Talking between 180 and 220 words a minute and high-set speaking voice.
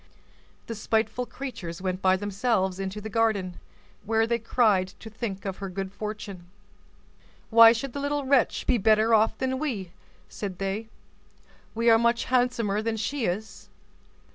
No: average, 155 wpm; high, 220 Hz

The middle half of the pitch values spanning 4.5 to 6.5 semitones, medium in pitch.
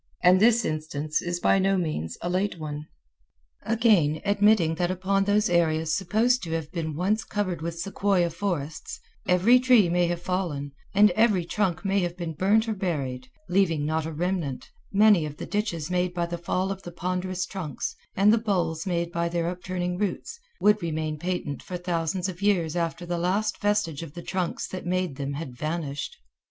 No: average, 3.3 semitones; medium, 175 Hz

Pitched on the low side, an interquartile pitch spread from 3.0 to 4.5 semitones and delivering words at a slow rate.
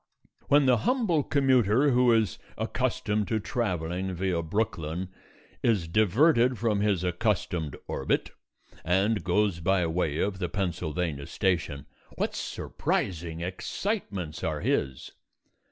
No: very low, 95 Hz; average, 5.1 semitones; slow, 115 wpm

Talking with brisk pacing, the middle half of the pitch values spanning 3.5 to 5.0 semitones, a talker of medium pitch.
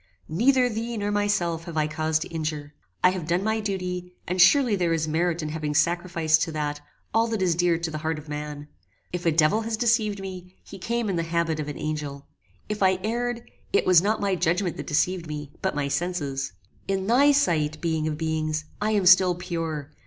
Yes: fast, 210 wpm; average, 4.4 semitones; medium, 175 Hz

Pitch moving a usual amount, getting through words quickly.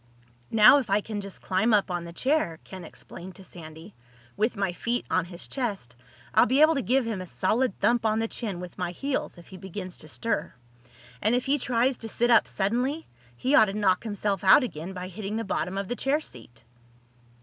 Yes: average, 4.7 semitones; fast, 215 wpm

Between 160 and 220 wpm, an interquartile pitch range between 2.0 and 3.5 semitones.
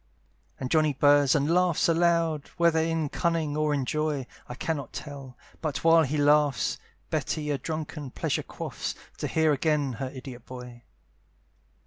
No: average, 150 wpm; narrow, 2.6 semitones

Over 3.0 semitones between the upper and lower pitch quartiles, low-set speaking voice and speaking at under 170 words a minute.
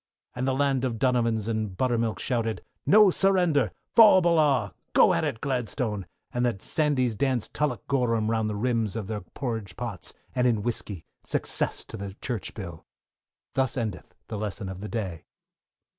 Yes: average, 3.9 semitones; low, 115 Hz; average, 160 wpm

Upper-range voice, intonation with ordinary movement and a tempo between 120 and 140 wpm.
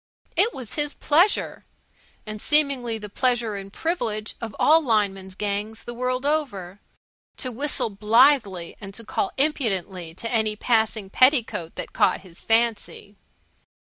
Yes: high, 225 Hz; average, 4.8 semitones; slow, 135 wpm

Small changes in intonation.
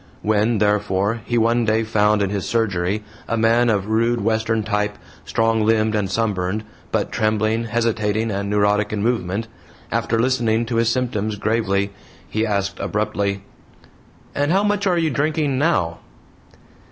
Yes: narrow, 2.0 semitones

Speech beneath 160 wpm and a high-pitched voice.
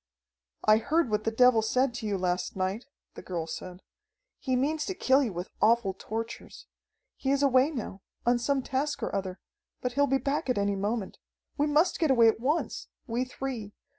No: average, 195 wpm; high, 240 Hz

